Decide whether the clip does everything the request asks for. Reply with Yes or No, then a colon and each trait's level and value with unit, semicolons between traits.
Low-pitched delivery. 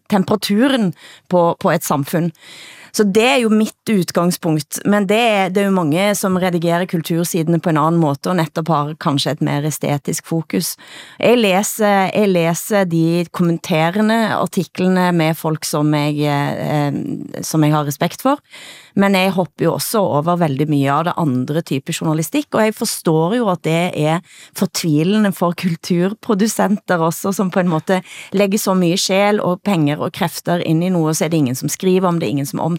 No: medium, 175 Hz